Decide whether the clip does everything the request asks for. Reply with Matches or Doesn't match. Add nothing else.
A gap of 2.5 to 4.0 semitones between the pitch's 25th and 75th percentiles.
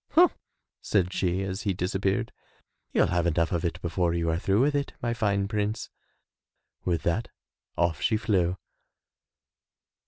Matches